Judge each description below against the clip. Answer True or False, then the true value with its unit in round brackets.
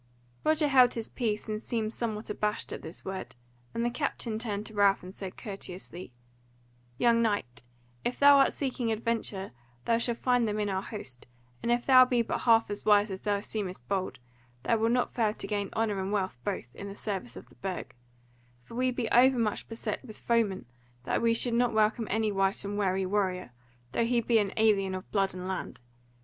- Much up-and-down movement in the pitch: False (3.2 semitones)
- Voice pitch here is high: True (215 Hz)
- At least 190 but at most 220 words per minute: True (200 wpm)